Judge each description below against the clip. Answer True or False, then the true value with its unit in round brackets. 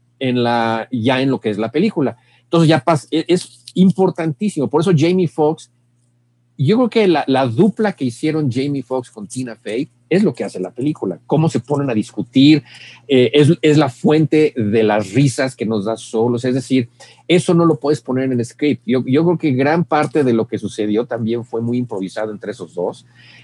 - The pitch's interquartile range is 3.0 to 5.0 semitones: True (4.5 semitones)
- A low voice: True (130 Hz)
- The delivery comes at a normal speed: False (205 wpm)